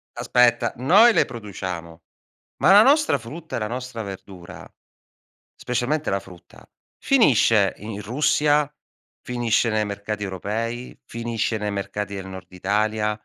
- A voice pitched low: Yes, low, 110 Hz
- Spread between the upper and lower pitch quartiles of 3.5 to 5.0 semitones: Yes, average, 3.9 semitones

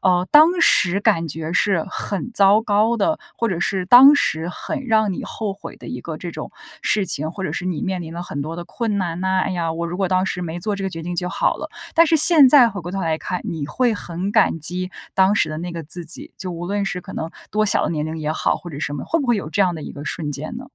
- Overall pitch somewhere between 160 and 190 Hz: Yes, medium, 185 Hz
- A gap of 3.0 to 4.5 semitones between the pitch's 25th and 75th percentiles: Yes, average, 4.0 semitones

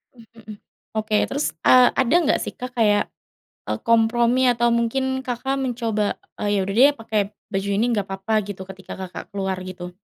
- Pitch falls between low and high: No, high, 225 Hz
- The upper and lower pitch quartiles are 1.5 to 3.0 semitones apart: No, average, 3.4 semitones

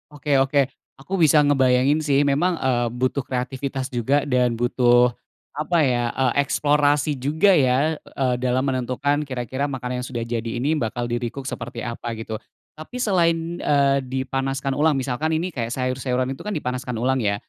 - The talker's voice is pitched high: No, low, 130 Hz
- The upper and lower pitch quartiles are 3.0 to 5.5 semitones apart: No, narrow, 2.6 semitones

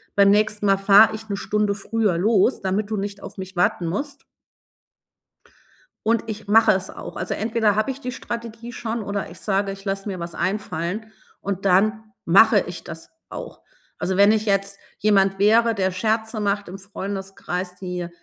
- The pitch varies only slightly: Yes, narrow, 2.2 semitones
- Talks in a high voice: Yes, high, 200 Hz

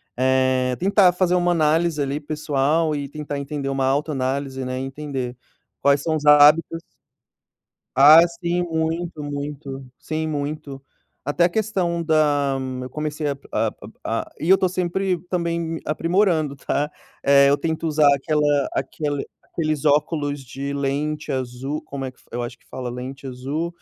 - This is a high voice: No, medium, 150 Hz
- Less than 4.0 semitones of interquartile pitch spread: Yes, average, 2.9 semitones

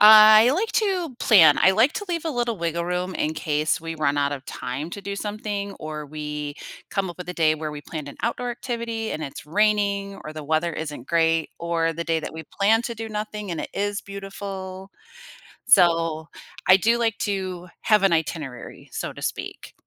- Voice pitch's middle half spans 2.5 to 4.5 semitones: No, average, 5.1 semitones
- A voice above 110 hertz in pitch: Yes, medium, 185 Hz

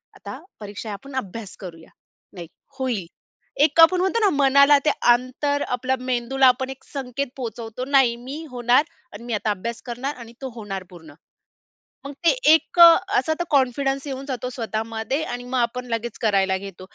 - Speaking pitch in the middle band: No, very high, 250 Hz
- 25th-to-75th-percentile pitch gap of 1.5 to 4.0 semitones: Yes, average, 3.6 semitones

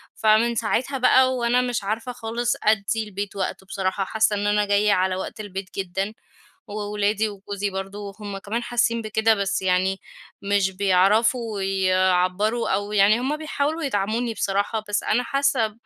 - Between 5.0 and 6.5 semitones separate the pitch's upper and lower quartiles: No, average, 2.9 semitones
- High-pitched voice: Yes, high, 210 Hz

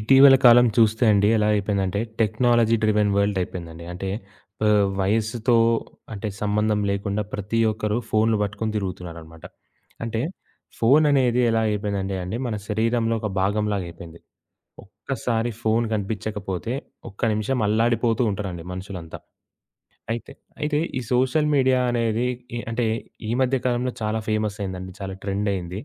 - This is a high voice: No, low, 105 Hz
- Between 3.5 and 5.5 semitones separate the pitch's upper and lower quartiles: No, average, 2.8 semitones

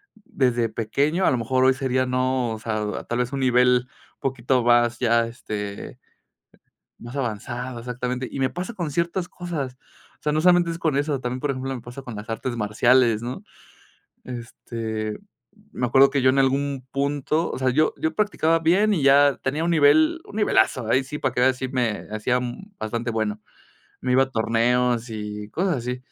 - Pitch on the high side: No, low, 130 Hz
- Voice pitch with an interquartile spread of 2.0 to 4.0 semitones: Yes, average, 3.1 semitones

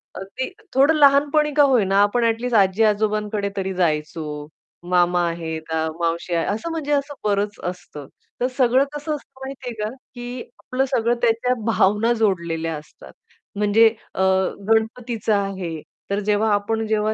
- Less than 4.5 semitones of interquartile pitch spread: No, average, 5.2 semitones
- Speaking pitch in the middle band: No, high, 210 Hz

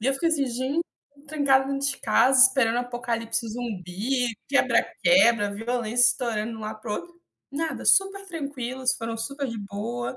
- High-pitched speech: Yes, high, 245 Hz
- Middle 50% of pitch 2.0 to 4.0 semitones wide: Yes, average, 3.4 semitones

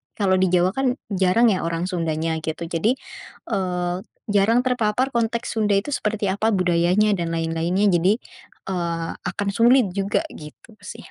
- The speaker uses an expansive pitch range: No, average, 3.8 semitones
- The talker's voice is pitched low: No, high, 190 Hz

